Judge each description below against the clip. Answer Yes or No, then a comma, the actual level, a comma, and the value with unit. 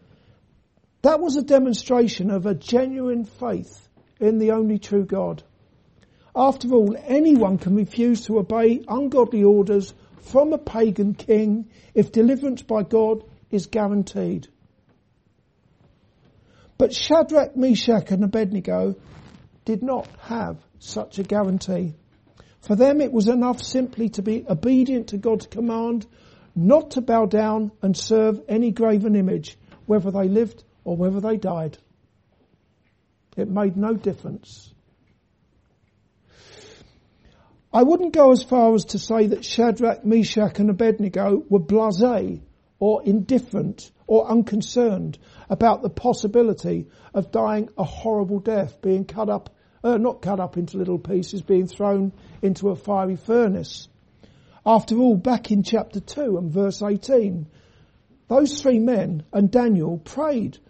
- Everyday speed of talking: No, slow, 130 wpm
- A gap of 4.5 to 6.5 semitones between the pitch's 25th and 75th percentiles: No, average, 3.3 semitones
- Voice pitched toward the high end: Yes, high, 210 Hz